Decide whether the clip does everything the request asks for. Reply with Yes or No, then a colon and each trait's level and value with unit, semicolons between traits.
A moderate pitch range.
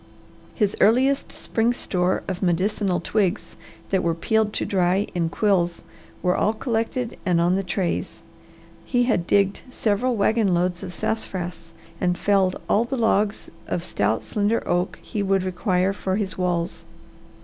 Yes: average, 3.5 semitones